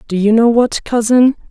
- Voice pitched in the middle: No, high, 230 Hz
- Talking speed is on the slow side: No, average, 200 wpm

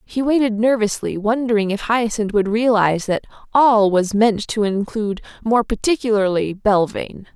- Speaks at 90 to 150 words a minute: Yes, average, 140 wpm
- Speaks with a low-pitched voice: No, high, 215 Hz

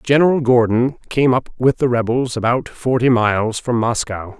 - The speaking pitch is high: No, low, 120 Hz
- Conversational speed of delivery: Yes, average, 165 wpm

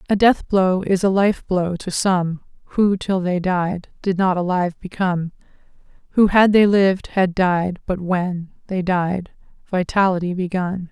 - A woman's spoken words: Yes, female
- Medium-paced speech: Yes, average, 160 wpm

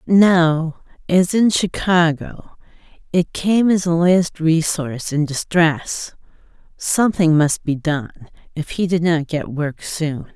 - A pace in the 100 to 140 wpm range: Yes, slow, 135 wpm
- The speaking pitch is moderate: Yes, medium, 165 Hz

